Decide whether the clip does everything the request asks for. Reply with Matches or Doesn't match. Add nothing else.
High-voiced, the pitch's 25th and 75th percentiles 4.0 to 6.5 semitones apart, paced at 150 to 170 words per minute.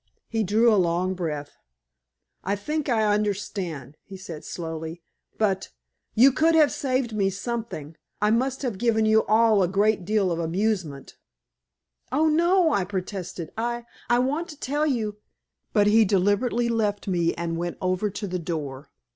Matches